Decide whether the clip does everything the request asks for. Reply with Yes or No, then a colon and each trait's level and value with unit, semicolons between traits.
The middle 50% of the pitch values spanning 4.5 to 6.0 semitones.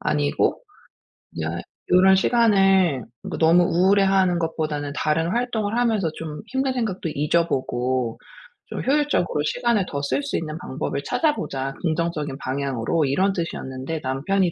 Yes: wide, 5.6 semitones